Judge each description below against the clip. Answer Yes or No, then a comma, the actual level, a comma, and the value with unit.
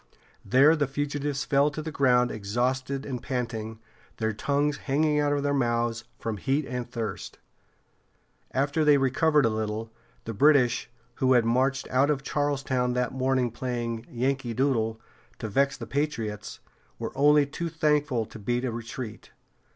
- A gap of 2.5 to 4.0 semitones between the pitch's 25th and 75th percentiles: Yes, average, 3.4 semitones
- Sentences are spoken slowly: No, average, 155 wpm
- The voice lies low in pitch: Yes, low, 130 Hz